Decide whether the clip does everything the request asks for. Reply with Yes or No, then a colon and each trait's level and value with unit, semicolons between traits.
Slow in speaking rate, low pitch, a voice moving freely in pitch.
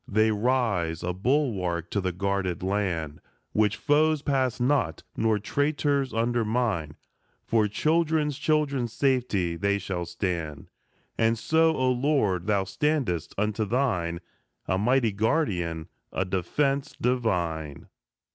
Yes: slow, 120 wpm; low, 110 Hz; wide, 6.7 semitones